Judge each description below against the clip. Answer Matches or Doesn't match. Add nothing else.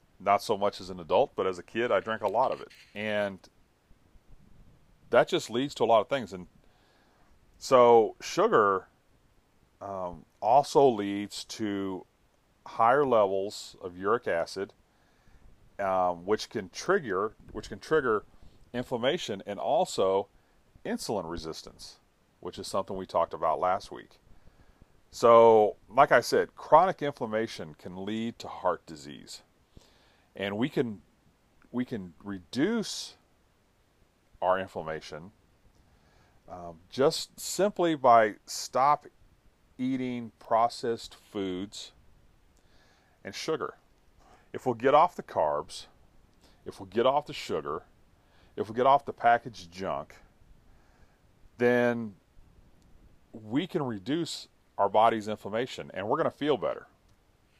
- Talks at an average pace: Doesn't match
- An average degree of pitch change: Matches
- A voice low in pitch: Matches